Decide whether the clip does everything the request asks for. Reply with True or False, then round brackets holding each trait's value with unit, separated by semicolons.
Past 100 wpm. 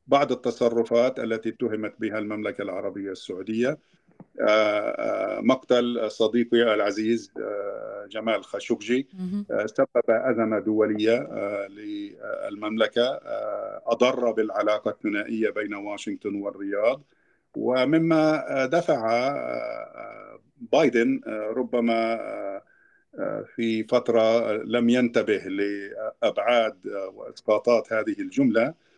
False (70 wpm)